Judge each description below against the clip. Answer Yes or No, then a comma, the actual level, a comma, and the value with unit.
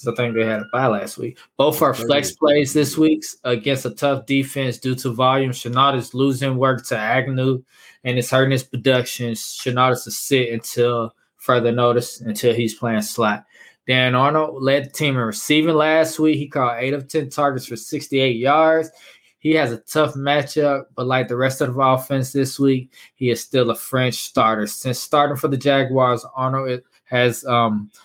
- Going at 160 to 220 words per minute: Yes, average, 190 wpm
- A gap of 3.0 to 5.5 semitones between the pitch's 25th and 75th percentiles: No, narrow, 2.4 semitones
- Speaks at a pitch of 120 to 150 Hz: Yes, low, 130 Hz